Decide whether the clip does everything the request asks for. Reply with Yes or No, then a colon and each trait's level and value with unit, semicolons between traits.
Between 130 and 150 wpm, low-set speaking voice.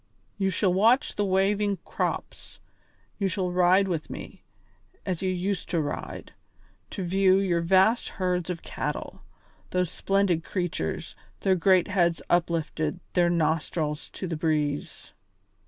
No: slow, 135 wpm; medium, 180 Hz